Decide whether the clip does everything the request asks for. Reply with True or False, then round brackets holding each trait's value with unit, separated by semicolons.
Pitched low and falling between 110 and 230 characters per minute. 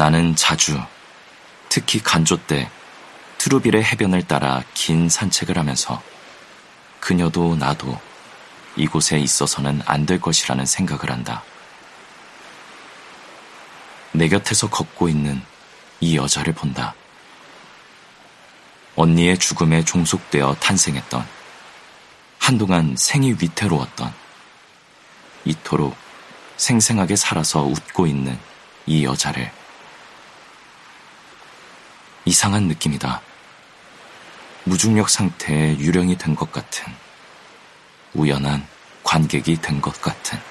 True (80 Hz; 200 characters per minute)